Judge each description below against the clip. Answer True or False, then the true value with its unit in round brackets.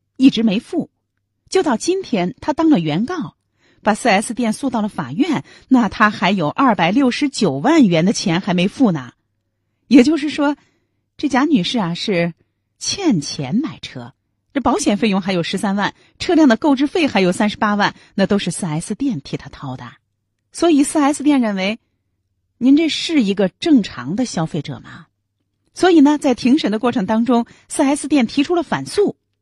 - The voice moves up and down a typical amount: False (8.5 semitones)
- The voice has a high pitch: True (220 Hz)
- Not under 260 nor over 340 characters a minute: False (250 characters per minute)